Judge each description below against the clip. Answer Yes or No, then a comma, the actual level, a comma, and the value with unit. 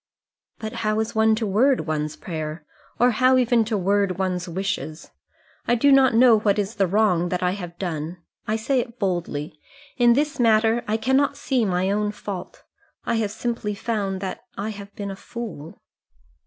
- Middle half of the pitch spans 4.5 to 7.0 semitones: No, average, 4.1 semitones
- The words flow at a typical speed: Yes, average, 180 wpm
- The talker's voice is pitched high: Yes, high, 210 Hz